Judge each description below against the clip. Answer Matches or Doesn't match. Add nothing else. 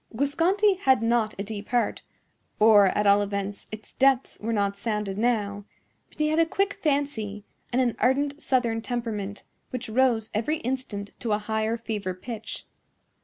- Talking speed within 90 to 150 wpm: Doesn't match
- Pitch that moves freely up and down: Doesn't match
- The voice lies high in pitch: Matches